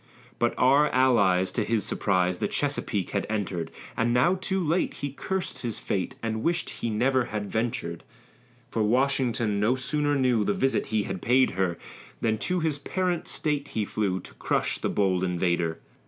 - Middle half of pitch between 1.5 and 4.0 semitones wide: No, wide, 5.6 semitones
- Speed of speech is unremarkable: Yes, average, 175 wpm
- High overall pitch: No, low, 115 Hz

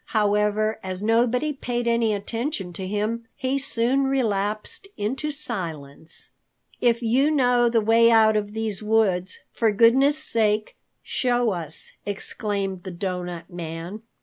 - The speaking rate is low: Yes, slow, 130 wpm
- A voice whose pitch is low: No, high, 220 Hz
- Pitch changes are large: No, average, 3.7 semitones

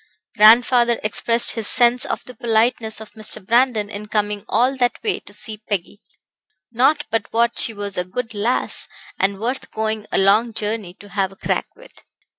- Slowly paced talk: No, average, 180 wpm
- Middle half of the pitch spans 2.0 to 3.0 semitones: Yes, narrow, 2.5 semitones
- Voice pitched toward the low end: No, high, 220 Hz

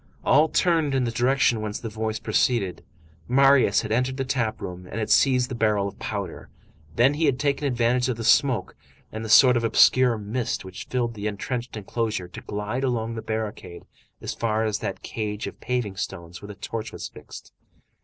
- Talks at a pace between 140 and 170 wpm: No, average, 195 wpm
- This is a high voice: No, low, 115 Hz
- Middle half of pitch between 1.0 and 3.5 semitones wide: Yes, average, 3.1 semitones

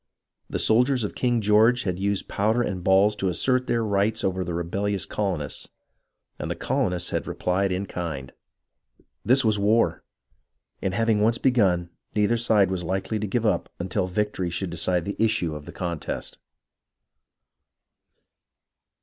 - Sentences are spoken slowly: No, average, 150 wpm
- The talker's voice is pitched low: Yes, low, 100 Hz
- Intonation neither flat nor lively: Yes, average, 3.6 semitones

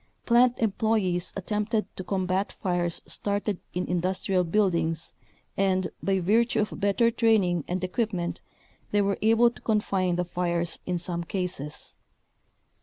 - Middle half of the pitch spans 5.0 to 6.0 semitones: No, average, 3.1 semitones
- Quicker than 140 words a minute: No, slow, 135 wpm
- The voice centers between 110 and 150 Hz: No, high, 190 Hz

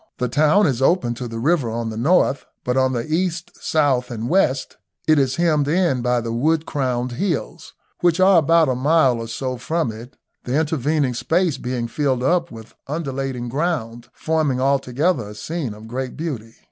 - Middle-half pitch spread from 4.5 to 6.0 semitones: Yes, average, 4.9 semitones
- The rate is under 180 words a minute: No, average, 185 wpm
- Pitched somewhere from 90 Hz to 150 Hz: Yes, low, 135 Hz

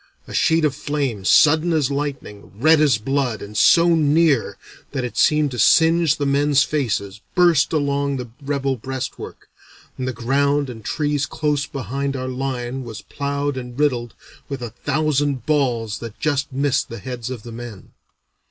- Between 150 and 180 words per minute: Yes, average, 165 wpm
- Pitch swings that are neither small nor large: Yes, average, 3.2 semitones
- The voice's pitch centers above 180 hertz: No, medium, 140 Hz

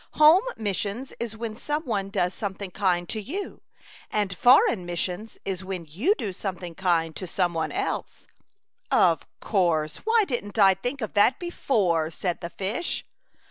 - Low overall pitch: No, high, 200 Hz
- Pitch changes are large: No, average, 4.8 semitones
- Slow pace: No, average, 165 wpm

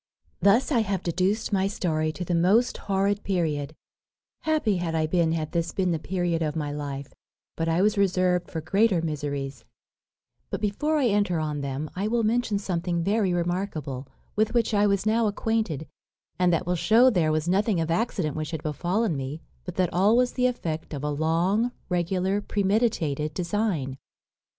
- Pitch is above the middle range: No, medium, 180 Hz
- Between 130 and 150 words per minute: No, average, 180 wpm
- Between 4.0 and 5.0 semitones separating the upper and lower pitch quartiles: Yes, average, 4.6 semitones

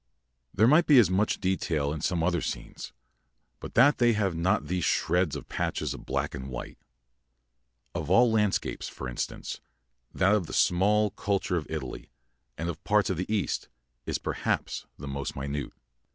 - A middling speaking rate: Yes, average, 175 wpm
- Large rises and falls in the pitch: Yes, wide, 5.9 semitones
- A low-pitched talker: Yes, very low, 90 Hz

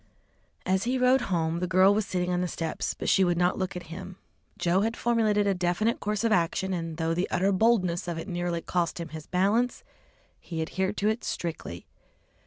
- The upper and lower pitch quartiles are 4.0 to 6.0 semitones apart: No, average, 3.1 semitones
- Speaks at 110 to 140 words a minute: No, fast, 205 wpm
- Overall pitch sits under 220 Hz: Yes, medium, 185 Hz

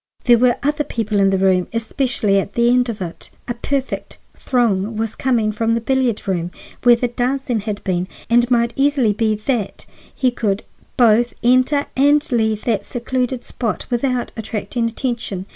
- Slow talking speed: No, average, 175 wpm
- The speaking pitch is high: Yes, high, 235 Hz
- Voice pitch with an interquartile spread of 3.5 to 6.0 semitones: No, average, 2.9 semitones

